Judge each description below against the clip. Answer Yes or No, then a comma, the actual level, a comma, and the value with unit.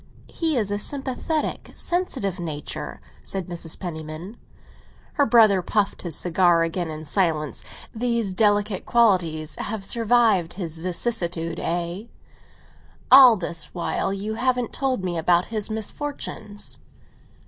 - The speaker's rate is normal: No, slow, 120 wpm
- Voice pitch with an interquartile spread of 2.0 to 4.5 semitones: No, average, 5.2 semitones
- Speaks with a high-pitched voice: Yes, high, 195 Hz